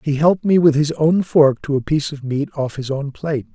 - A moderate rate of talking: No, fast, 270 wpm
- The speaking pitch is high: No, medium, 150 Hz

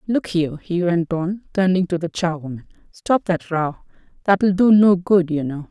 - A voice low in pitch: No, medium, 175 Hz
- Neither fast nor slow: Yes, average, 180 wpm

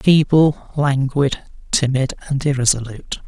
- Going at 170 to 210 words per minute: No, slow, 90 wpm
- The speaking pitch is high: No, medium, 140 Hz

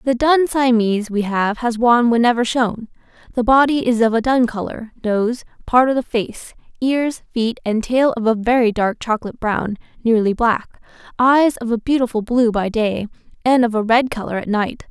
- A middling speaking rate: Yes, average, 190 wpm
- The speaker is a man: No, female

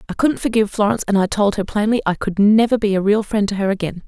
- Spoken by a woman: Yes, female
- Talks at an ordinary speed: No, fast, 280 wpm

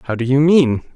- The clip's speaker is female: No, male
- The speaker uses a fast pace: Yes, fast, 250 wpm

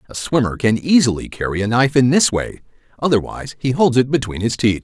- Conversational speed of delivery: No, fast, 210 wpm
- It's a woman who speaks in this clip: No, male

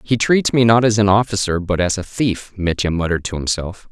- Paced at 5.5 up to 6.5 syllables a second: Yes, 5.6 syllables/s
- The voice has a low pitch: Yes, low, 100 Hz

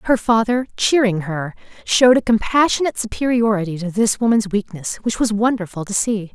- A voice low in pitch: No, high, 215 Hz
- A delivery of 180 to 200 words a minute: No, average, 160 wpm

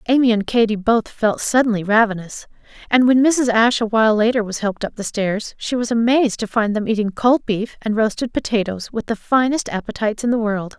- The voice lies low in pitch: No, high, 225 Hz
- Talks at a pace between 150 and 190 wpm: No, fast, 205 wpm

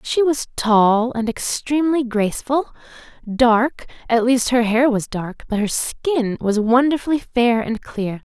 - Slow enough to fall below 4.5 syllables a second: Yes, 4.0 syllables/s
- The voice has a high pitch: Yes, high, 240 Hz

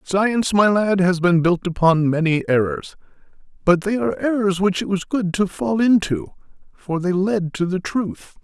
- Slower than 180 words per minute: No, average, 185 wpm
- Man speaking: Yes, male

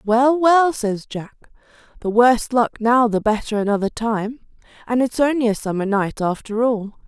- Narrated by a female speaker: Yes, female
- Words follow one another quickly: No, average, 170 wpm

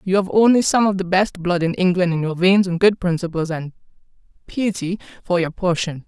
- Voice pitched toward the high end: No, medium, 180 Hz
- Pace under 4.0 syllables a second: No, 5.5 syllables/s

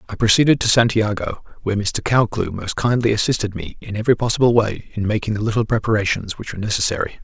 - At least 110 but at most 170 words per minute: No, average, 190 wpm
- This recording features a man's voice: Yes, male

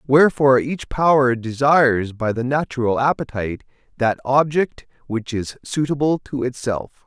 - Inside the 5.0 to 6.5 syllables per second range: No, 4.8 syllables/s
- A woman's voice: No, male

